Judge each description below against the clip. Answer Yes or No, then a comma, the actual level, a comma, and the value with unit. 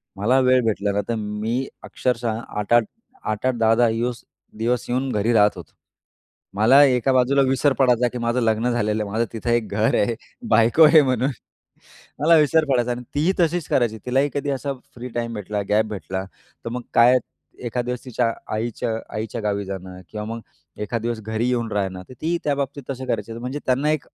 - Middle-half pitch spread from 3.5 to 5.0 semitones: No, average, 3.0 semitones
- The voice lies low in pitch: Yes, low, 120 Hz